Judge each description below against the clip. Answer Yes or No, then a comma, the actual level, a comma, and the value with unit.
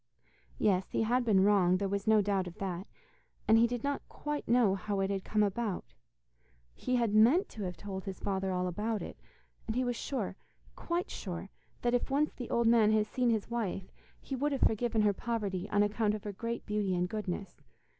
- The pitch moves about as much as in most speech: Yes, average, 3.4 semitones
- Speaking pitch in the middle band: No, high, 210 Hz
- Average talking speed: No, fast, 210 wpm